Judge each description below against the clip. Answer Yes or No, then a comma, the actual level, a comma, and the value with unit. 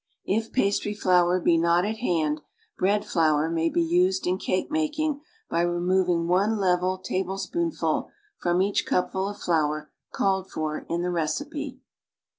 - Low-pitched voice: No, medium, 185 Hz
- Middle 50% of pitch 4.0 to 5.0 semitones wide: No, average, 3.1 semitones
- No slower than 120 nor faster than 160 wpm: Yes, average, 145 wpm